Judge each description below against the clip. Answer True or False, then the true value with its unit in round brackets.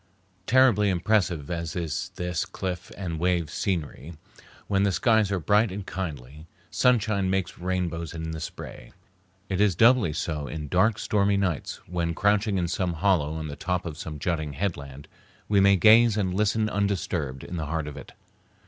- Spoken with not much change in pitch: False (4.0 semitones)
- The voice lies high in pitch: False (90 Hz)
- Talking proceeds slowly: False (170 wpm)